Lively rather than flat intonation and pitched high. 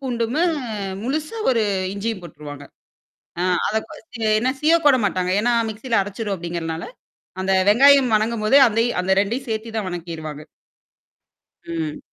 Yes: wide, 5.9 semitones; high, 220 Hz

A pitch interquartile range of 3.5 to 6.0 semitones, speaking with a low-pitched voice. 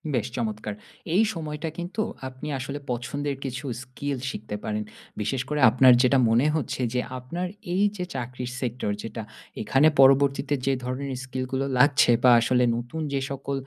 No: narrow, 2.4 semitones; low, 130 Hz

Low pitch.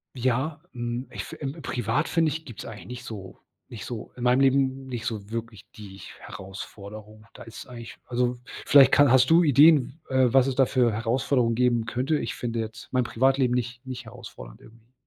Yes: low, 125 Hz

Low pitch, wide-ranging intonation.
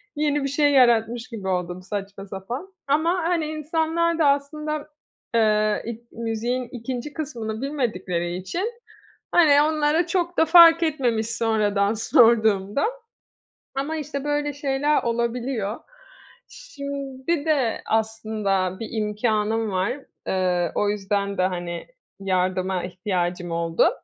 No: high, 235 Hz; wide, 6.6 semitones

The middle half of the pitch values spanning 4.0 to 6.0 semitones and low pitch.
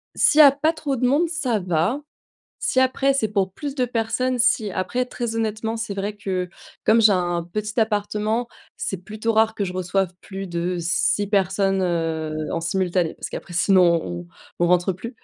No: average, 4.4 semitones; high, 205 Hz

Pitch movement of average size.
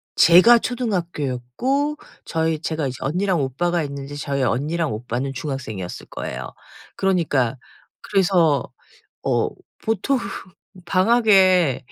No: wide, 6.1 semitones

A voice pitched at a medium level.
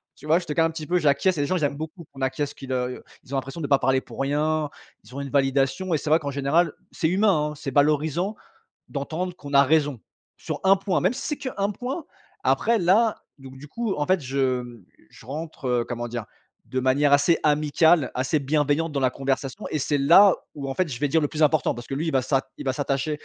Yes: medium, 145 Hz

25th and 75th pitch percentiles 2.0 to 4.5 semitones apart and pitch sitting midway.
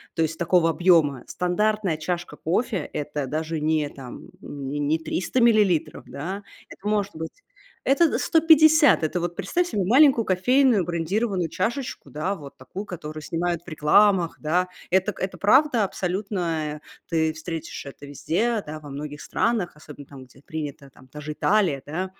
No: average, 5.3 semitones; medium, 175 Hz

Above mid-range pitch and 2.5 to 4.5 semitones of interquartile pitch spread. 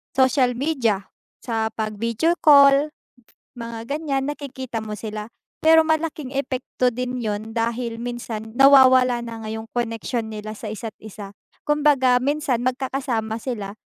Yes: high, 245 Hz; average, 3.5 semitones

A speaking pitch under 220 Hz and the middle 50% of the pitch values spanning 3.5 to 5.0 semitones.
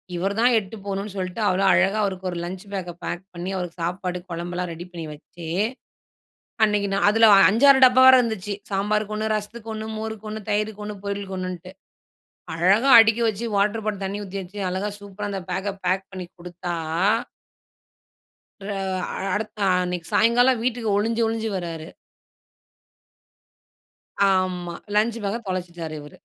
No: high, 195 Hz; average, 3.1 semitones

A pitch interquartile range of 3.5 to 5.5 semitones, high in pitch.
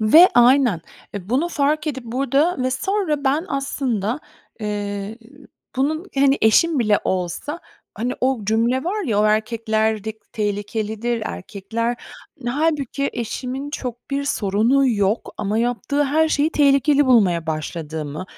Yes: average, 4.8 semitones; high, 240 Hz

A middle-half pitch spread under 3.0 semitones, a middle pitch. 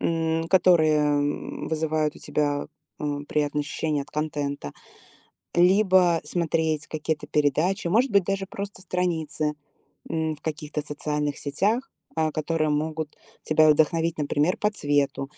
Yes: narrow, 2.5 semitones; medium, 155 Hz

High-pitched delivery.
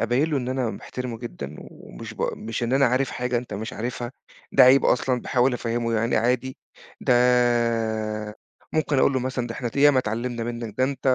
No: low, 125 Hz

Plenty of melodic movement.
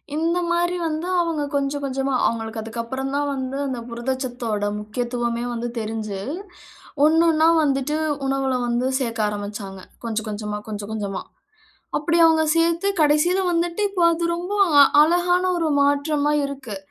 Yes: wide, 5.7 semitones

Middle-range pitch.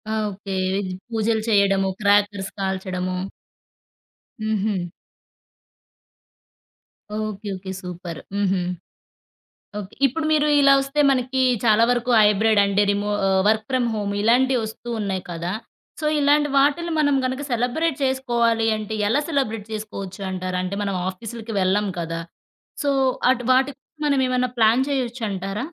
No: high, 215 Hz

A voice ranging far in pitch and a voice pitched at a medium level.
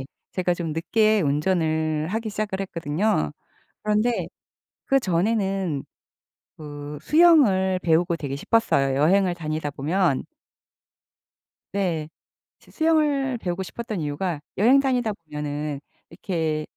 Yes: wide, 5.8 semitones; medium, 180 Hz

